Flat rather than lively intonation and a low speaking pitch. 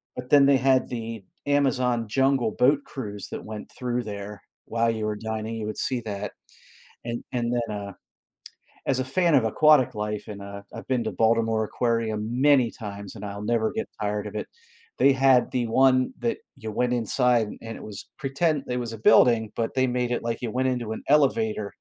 No: average, 3.1 semitones; low, 115 Hz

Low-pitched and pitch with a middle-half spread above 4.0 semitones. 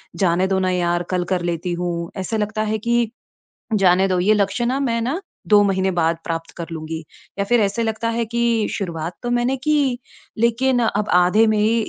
No: high, 210 Hz; average, 4.5 semitones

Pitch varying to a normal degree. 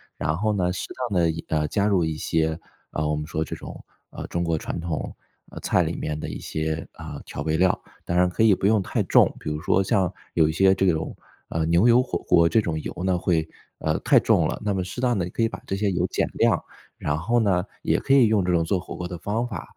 Yes: average, 3.7 semitones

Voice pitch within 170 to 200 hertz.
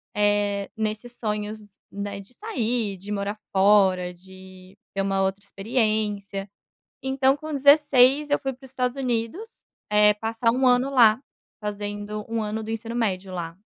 No: high, 215 Hz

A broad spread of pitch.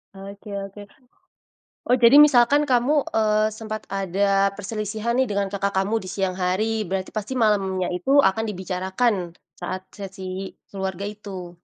No: narrow, 2.5 semitones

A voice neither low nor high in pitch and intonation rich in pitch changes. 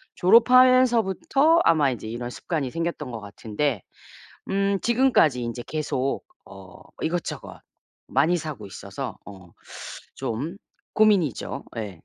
Yes: medium, 155 Hz; wide, 8.8 semitones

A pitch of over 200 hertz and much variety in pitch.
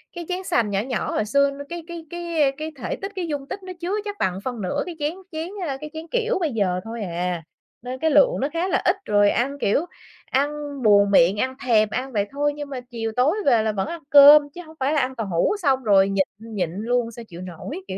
Yes: very high, 260 Hz; wide, 7.2 semitones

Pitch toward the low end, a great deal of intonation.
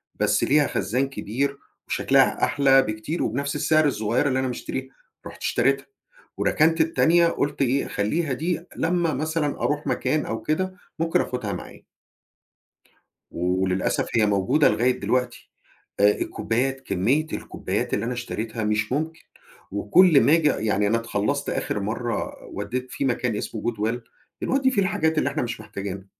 Yes: low, 130 Hz; wide, 5.9 semitones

